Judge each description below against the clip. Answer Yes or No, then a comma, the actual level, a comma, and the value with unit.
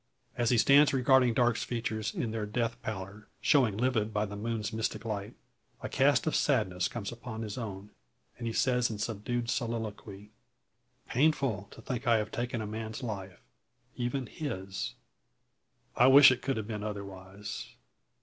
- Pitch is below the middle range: Yes, low, 110 Hz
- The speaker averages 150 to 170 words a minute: Yes, average, 160 wpm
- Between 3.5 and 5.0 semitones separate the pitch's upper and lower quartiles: No, average, 2.8 semitones